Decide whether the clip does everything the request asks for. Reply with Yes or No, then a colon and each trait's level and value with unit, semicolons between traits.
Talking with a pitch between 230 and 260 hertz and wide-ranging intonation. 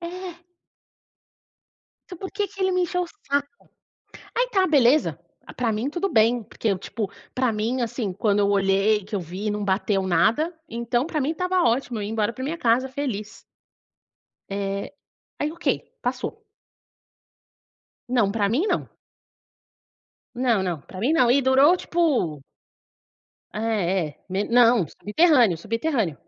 Yes: high, 235 Hz; wide, 6.8 semitones